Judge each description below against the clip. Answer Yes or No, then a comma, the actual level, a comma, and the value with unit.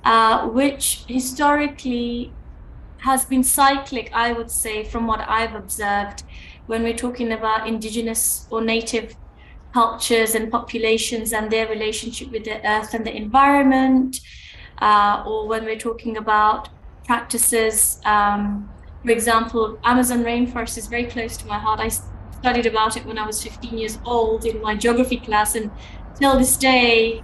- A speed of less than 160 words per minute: Yes, average, 150 wpm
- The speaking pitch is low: No, high, 230 Hz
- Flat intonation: Yes, narrow, 1.6 semitones